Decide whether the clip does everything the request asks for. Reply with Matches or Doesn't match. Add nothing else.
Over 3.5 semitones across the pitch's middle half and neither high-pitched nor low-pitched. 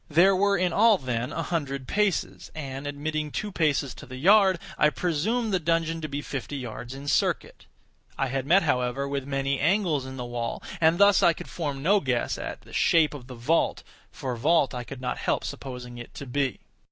Matches